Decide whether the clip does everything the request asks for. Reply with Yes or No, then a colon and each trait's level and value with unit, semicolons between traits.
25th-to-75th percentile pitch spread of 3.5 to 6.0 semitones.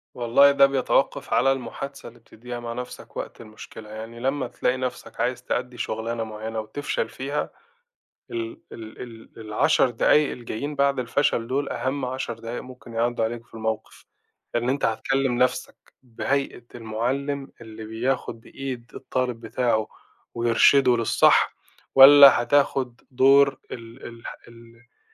No: average, 2.8 semitones